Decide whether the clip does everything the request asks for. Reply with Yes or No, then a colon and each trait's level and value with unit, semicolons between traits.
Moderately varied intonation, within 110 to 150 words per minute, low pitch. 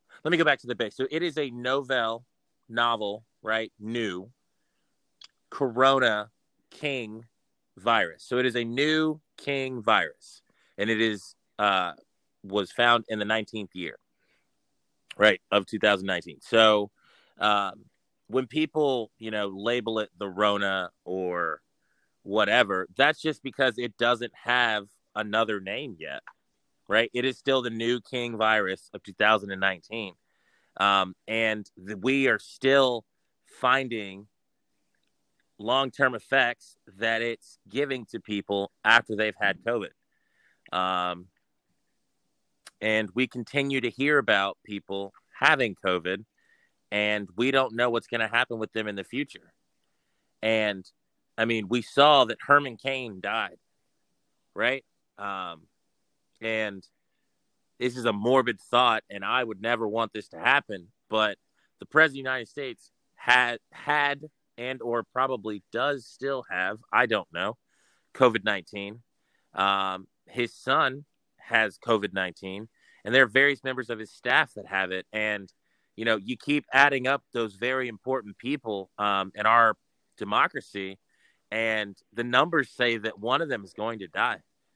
Yes: average, 4.0 semitones; average, 140 wpm; low, 115 Hz